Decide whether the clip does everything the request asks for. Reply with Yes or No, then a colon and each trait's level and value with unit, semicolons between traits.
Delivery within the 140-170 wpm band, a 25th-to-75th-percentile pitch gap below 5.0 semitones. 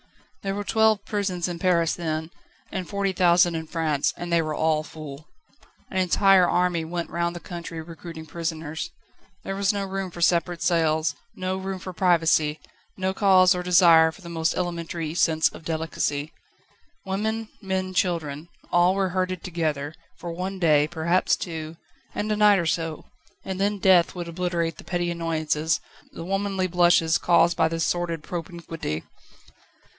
Yes: average, 160 wpm; narrow, 2.4 semitones